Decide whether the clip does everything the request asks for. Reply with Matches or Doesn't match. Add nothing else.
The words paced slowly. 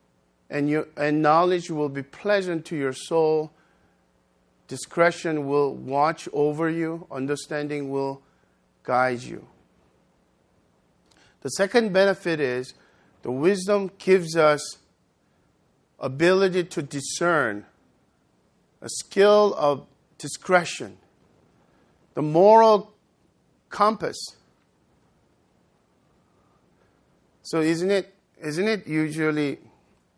Matches